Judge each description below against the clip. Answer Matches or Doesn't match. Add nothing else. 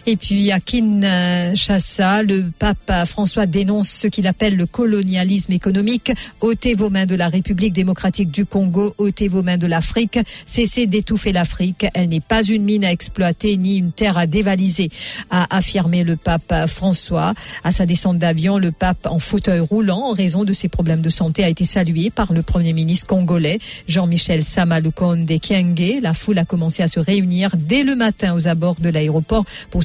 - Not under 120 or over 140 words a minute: Doesn't match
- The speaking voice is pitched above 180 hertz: Matches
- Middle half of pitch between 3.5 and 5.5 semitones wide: Doesn't match